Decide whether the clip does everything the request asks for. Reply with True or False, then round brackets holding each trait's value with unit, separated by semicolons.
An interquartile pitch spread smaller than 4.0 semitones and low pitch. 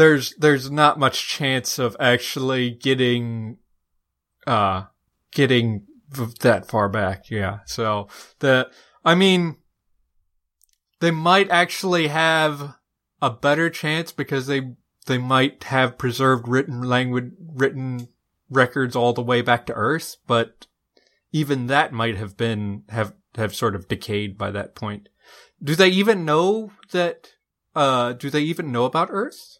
False (5.1 semitones; 130 Hz)